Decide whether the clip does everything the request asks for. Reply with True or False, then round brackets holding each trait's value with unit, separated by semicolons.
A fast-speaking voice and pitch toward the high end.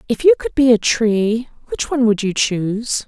True (215 wpm; 230 Hz)